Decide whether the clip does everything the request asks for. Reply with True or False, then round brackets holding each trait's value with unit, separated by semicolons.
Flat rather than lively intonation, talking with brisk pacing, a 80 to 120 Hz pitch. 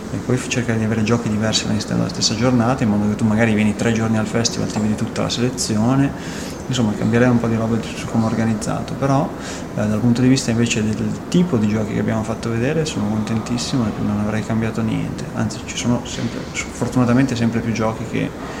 True (2.0 semitones; 225 wpm; 115 Hz)